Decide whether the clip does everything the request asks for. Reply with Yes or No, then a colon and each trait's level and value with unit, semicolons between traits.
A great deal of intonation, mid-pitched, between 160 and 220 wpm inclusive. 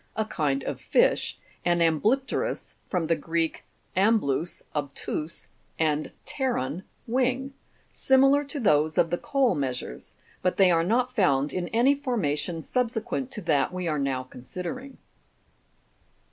No: wide, 8.6 semitones; medium, 180 Hz; slow, 135 wpm